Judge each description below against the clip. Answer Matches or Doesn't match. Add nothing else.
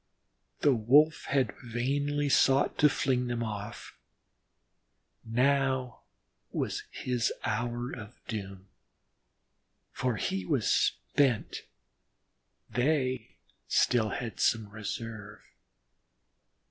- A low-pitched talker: Matches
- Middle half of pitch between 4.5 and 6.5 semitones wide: Doesn't match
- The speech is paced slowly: Matches